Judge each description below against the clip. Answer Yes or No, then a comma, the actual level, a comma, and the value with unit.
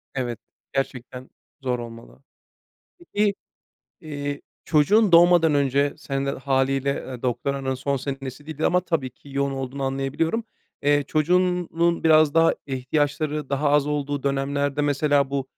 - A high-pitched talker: No, medium, 140 Hz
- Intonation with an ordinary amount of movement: No, narrow, 2.3 semitones